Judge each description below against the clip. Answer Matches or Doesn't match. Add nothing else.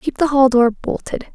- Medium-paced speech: Doesn't match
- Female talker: Matches